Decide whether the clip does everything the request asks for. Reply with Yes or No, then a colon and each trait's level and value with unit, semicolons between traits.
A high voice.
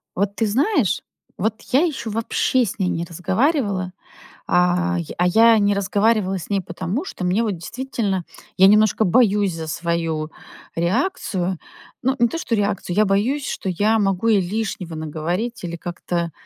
Yes: high, 195 Hz